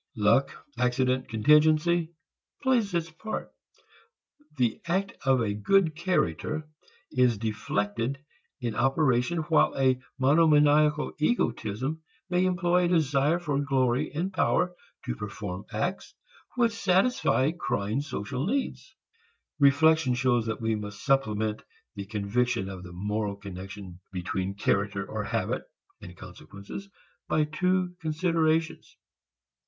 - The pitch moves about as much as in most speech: No, wide, 7.5 semitones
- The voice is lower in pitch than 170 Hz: Yes, low, 135 Hz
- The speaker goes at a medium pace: No, slow, 115 wpm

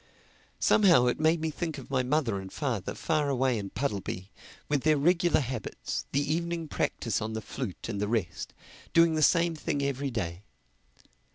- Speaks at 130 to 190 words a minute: Yes, average, 170 wpm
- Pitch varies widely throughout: Yes, wide, 6.1 semitones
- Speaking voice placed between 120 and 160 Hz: Yes, medium, 140 Hz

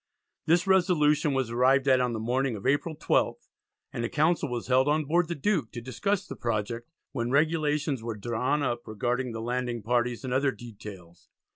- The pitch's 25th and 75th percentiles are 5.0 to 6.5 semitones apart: No, average, 4.1 semitones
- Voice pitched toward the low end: Yes, low, 130 Hz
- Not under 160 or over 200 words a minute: Yes, average, 185 wpm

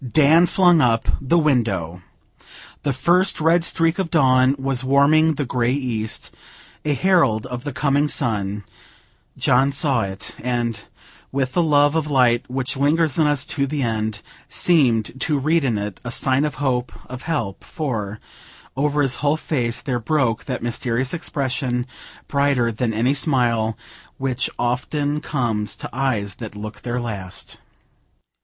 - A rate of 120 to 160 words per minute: Yes, average, 150 wpm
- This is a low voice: Yes, low, 130 Hz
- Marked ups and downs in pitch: No, average, 3.9 semitones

